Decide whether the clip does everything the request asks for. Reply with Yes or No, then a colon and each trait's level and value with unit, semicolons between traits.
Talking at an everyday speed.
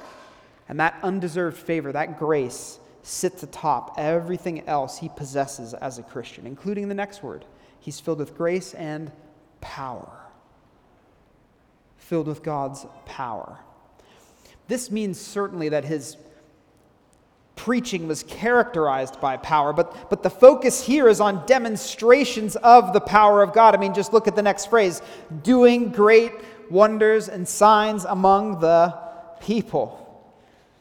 No: slow, 130 wpm